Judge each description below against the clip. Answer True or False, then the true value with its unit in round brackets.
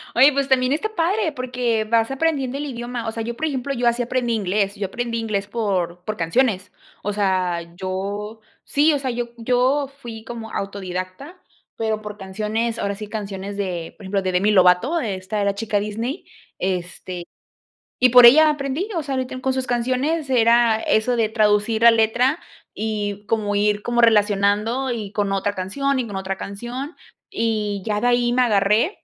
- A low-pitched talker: False (225 Hz)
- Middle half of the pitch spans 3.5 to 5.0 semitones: True (3.9 semitones)